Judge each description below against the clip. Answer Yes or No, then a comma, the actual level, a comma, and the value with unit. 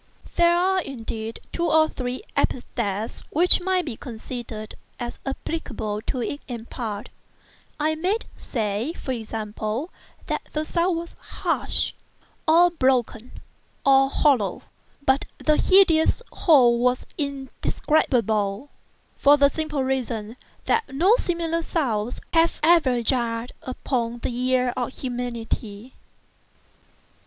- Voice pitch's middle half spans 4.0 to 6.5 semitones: Yes, wide, 5.5 semitones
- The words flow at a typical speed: No, slow, 115 wpm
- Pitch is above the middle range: Yes, very high, 260 Hz